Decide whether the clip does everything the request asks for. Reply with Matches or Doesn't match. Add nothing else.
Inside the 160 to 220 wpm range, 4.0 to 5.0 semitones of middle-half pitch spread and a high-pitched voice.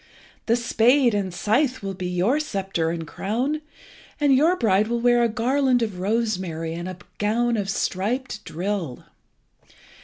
Doesn't match